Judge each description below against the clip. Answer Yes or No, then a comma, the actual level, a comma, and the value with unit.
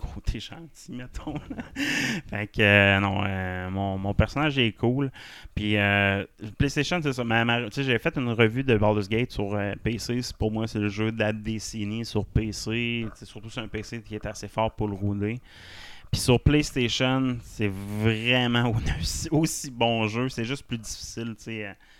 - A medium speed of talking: Yes, average, 190 wpm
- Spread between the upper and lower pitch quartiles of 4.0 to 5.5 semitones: No, average, 2.9 semitones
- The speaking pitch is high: No, low, 110 Hz